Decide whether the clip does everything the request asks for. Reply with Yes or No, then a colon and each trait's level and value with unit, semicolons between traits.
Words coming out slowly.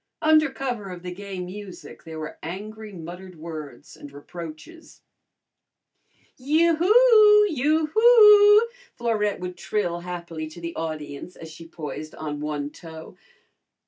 Yes: slow, 130 wpm